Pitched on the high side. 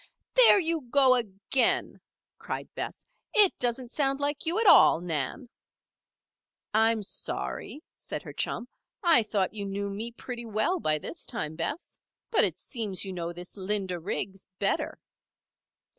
Yes: high, 220 Hz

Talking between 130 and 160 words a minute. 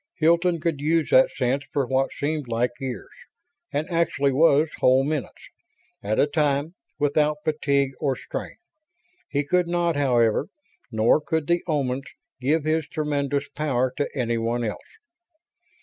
Yes: average, 140 wpm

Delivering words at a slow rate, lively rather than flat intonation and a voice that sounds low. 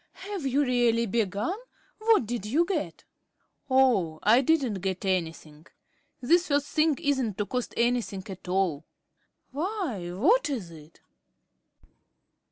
No: slow, 125 wpm; wide, 7.2 semitones; high, 235 Hz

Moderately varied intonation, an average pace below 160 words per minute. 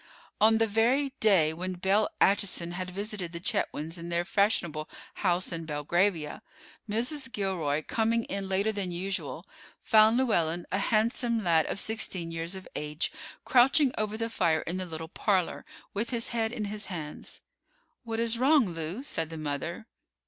No: average, 4.8 semitones; average, 165 wpm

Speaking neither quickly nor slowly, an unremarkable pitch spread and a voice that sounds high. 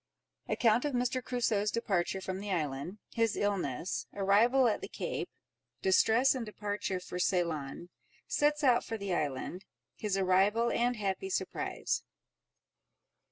No: slow, 110 wpm; average, 4.4 semitones; high, 205 Hz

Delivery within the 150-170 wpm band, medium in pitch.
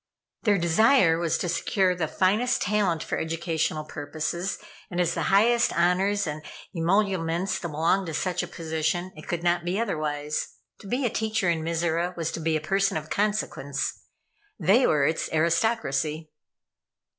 Yes: average, 155 wpm; medium, 170 Hz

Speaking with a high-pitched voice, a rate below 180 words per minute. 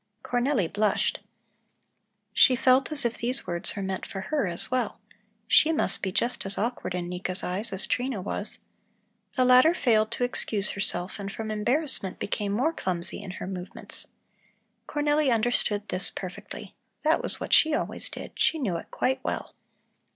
Yes: high, 215 Hz; average, 165 wpm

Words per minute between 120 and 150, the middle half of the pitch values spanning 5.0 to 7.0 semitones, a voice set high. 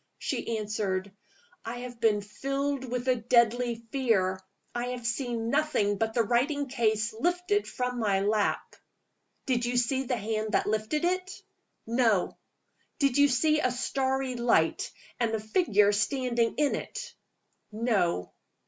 No: average, 140 wpm; average, 3.4 semitones; high, 240 Hz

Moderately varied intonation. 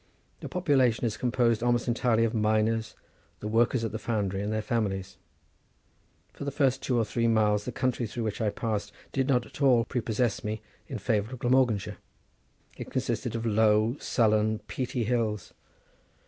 No: narrow, 2.3 semitones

